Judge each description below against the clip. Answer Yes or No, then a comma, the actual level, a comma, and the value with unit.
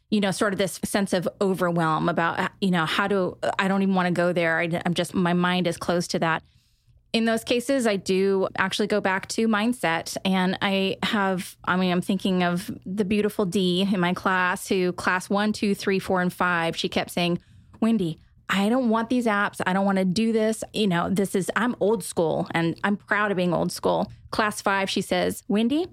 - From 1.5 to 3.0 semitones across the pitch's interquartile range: Yes, average, 2.7 semitones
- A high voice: Yes, high, 195 Hz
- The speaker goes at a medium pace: No, fast, 220 wpm